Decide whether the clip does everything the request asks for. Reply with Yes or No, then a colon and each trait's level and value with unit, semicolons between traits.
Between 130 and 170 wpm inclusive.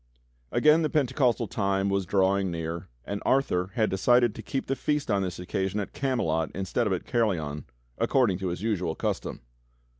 No: average, 180 wpm